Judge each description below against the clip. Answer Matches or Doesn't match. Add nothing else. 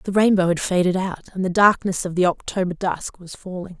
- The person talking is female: Matches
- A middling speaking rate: Doesn't match